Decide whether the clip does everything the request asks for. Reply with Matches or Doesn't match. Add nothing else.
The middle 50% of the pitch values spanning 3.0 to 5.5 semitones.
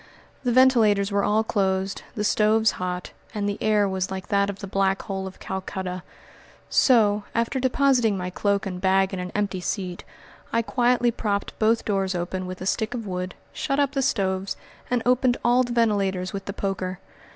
Matches